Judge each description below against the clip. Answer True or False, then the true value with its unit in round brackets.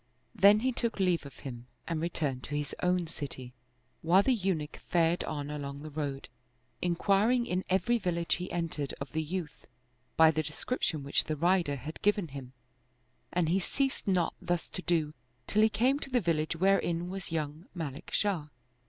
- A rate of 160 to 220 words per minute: True (180 wpm)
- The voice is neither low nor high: True (170 Hz)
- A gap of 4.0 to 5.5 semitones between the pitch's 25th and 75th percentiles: True (4.3 semitones)